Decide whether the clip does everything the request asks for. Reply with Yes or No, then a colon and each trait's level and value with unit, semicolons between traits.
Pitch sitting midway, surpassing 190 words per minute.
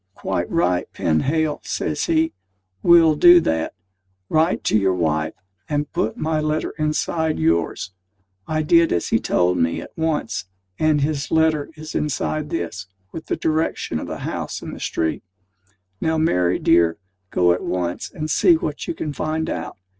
No: medium, 150 Hz; average, 160 wpm